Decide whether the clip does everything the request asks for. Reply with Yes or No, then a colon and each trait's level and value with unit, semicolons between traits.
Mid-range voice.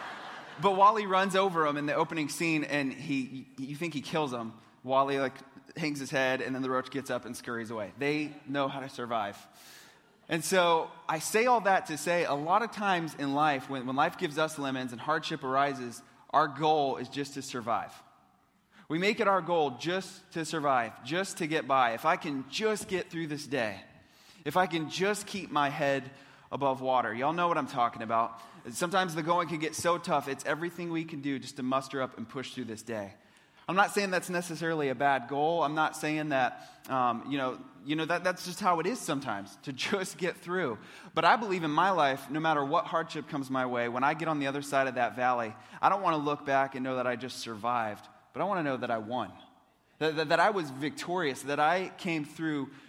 Yes: medium, 150 Hz